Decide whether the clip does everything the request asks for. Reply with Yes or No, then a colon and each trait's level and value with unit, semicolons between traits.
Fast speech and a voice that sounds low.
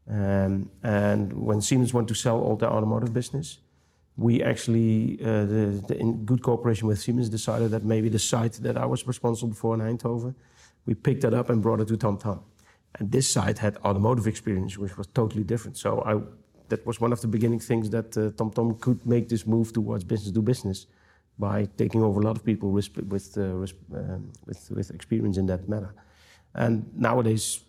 Yes: fast, 205 wpm; low, 110 Hz